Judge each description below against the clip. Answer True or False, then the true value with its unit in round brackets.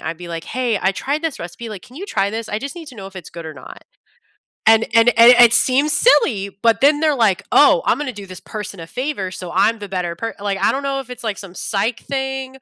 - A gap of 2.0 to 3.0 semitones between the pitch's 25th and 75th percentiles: False (5.5 semitones)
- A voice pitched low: False (225 Hz)